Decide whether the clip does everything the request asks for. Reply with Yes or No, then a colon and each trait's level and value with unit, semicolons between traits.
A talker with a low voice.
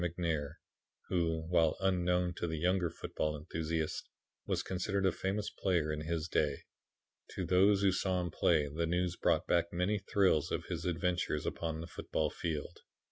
Yes: very low, 85 Hz